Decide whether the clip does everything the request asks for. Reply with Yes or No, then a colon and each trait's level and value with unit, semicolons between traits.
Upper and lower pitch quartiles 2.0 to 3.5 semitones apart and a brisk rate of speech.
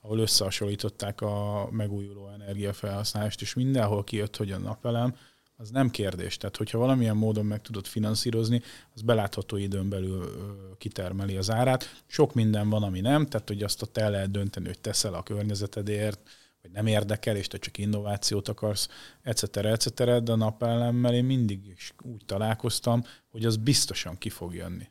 Yes: narrow, 2.4 semitones; fast, 165 wpm